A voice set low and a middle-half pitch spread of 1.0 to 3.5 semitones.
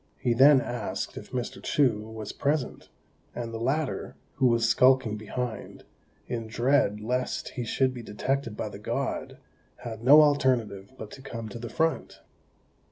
Yes: low, 120 Hz; average, 3.0 semitones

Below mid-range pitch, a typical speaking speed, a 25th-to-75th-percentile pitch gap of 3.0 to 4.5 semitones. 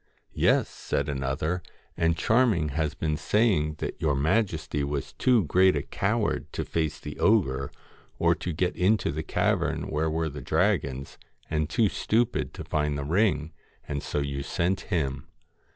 Yes: very low, 80 Hz; average, 170 wpm; average, 4.1 semitones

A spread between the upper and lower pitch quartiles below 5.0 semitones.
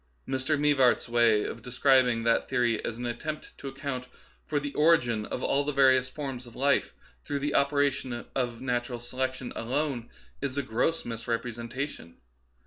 Yes: average, 2.8 semitones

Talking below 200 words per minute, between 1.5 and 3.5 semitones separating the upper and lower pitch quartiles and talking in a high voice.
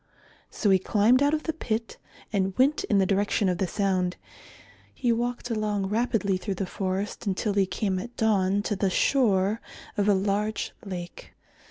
Yes: average, 175 wpm; average, 3.0 semitones; high, 205 Hz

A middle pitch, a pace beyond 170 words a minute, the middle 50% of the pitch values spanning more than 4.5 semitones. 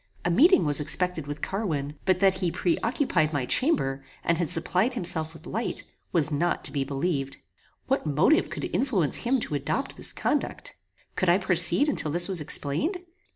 Yes: medium, 175 Hz; average, 180 wpm; average, 5.1 semitones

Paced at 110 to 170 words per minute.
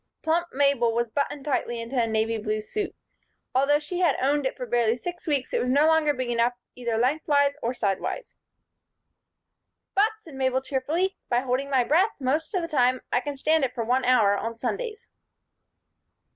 No: average, 185 wpm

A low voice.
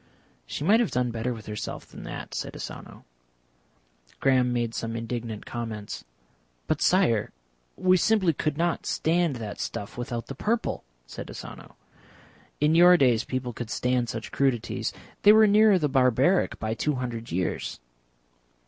Yes: low, 125 Hz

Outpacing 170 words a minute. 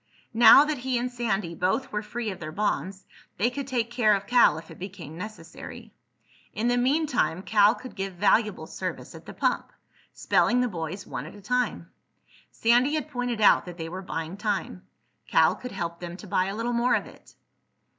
Yes: average, 195 wpm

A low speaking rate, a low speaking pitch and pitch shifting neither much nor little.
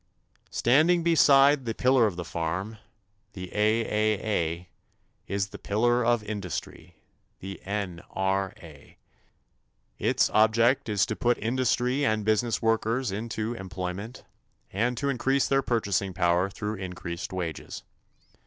Yes: slow, 115 wpm; low, 110 Hz; average, 4.1 semitones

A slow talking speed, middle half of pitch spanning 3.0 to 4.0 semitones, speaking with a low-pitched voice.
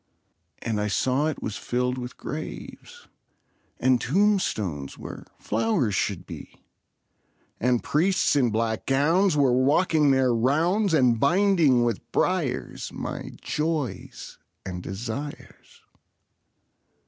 No: slow, 110 wpm; wide, 5.5 semitones; low, 130 Hz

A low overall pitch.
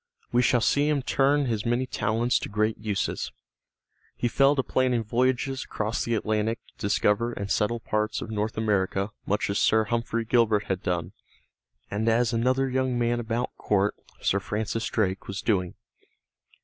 Yes: low, 115 Hz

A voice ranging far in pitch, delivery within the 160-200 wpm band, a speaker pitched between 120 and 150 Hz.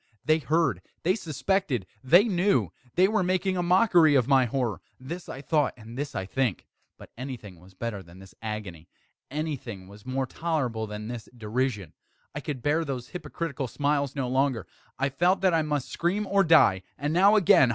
Yes: wide, 6.7 semitones; average, 185 wpm; low, 135 Hz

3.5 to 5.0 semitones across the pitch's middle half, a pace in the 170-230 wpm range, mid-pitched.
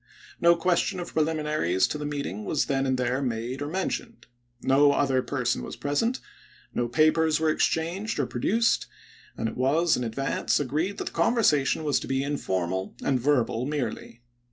Yes: average, 4.2 semitones; average, 180 wpm; medium, 145 Hz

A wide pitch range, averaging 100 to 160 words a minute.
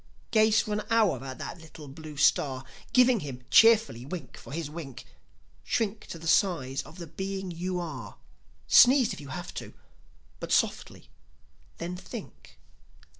Yes: wide, 6.7 semitones; average, 155 wpm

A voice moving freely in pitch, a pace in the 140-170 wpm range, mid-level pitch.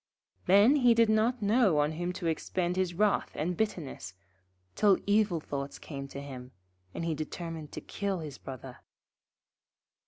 Yes: wide, 5.8 semitones; average, 155 wpm; medium, 175 Hz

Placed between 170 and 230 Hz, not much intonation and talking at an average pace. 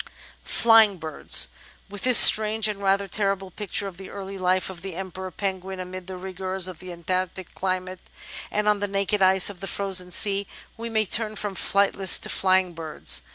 Yes: high, 190 Hz; narrow, 1.6 semitones; average, 190 wpm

